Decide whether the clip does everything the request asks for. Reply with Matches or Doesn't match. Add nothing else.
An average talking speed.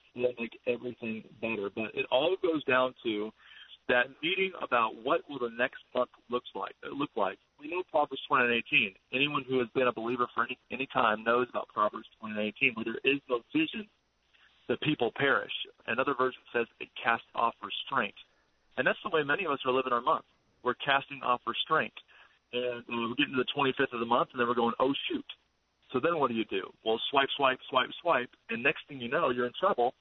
Doesn't match